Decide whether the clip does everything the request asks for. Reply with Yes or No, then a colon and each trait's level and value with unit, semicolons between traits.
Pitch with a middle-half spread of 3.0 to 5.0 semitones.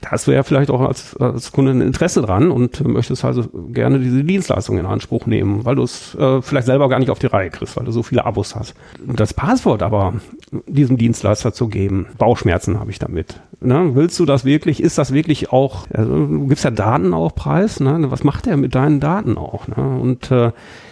Yes: average, 3.3 semitones